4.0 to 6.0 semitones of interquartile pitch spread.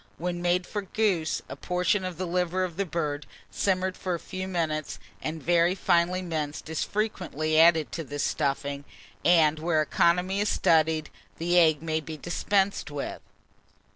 No: average, 2.7 semitones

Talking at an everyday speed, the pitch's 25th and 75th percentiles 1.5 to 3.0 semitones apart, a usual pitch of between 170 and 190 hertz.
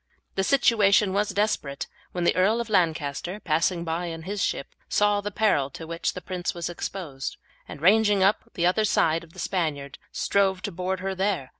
No: average, 195 wpm; average, 3.6 semitones; medium, 185 Hz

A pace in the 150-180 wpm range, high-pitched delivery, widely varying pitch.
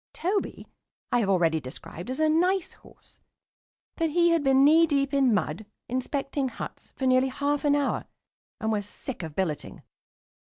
Yes: average, 165 wpm; very high, 270 Hz; wide, 6.5 semitones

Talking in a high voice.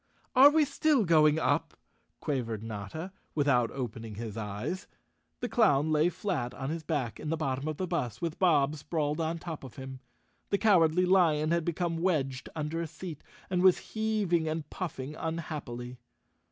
No: medium, 155 Hz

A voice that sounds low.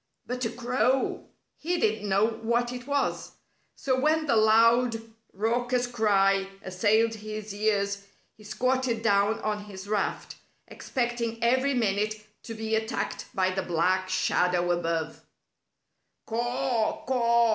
No: high, 220 Hz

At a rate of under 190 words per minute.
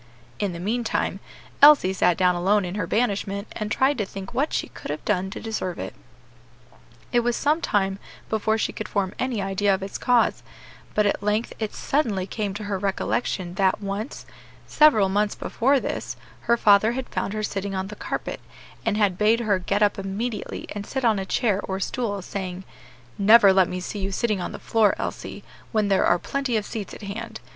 No: average, 200 wpm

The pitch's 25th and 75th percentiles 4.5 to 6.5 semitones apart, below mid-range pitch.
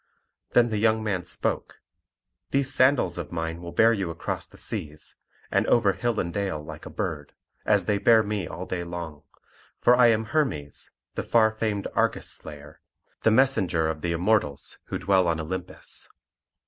Yes: average, 5.3 semitones; very low, 95 Hz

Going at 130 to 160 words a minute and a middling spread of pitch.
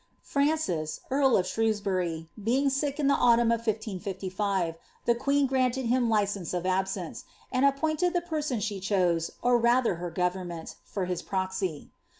No: average, 150 wpm; wide, 6.2 semitones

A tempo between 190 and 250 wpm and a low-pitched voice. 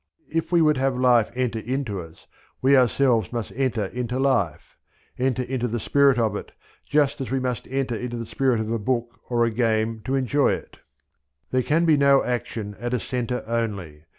Yes: average, 195 wpm; low, 125 Hz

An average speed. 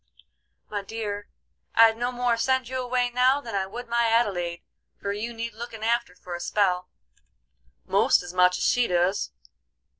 Yes: average, 170 wpm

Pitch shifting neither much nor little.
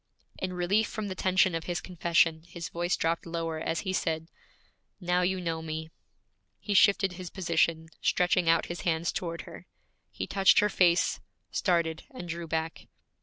No: narrow, 2.1 semitones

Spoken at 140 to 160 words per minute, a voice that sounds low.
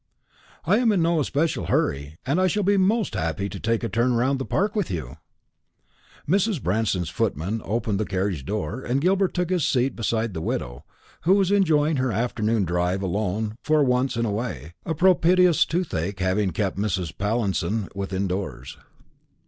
No: average, 175 wpm; low, 115 Hz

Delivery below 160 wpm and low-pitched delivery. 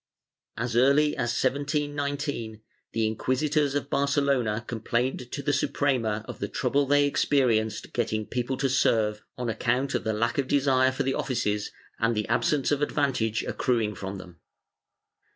Yes: average, 150 wpm; low, 130 Hz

